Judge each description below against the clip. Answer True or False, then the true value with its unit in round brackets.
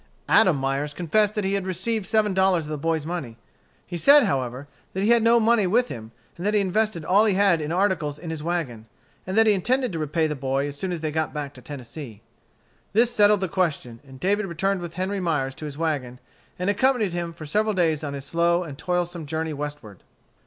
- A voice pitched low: False (170 Hz)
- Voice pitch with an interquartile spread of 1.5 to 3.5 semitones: False (5.1 semitones)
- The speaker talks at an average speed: False (225 wpm)